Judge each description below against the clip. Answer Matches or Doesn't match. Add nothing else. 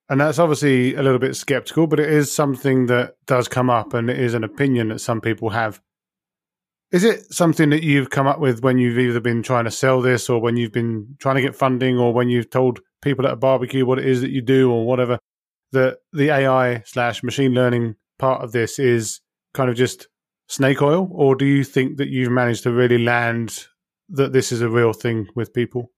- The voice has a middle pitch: Doesn't match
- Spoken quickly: Matches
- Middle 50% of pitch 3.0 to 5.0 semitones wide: Doesn't match